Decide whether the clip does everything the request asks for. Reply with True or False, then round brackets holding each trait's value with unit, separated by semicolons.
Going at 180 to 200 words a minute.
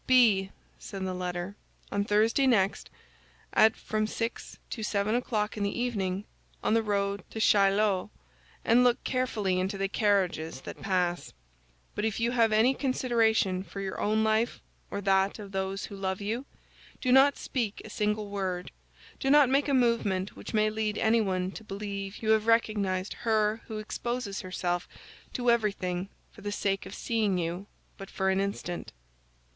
False (165 wpm)